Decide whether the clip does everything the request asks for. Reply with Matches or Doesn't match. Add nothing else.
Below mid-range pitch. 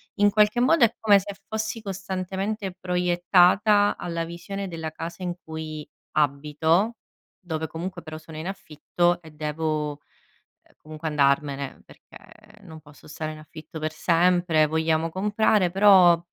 Doesn't match